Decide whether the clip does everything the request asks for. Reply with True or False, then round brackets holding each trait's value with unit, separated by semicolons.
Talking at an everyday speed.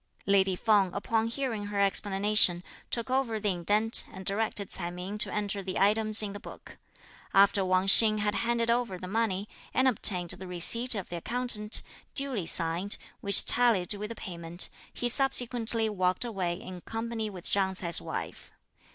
True (170 wpm)